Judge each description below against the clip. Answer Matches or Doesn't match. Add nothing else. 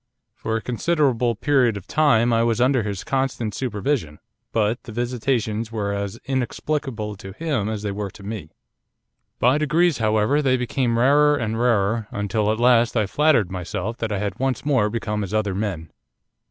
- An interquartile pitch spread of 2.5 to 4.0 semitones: Matches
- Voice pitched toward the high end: Doesn't match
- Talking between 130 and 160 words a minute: Doesn't match